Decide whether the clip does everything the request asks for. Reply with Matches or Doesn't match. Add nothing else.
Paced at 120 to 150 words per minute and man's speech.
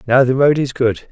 Doesn't match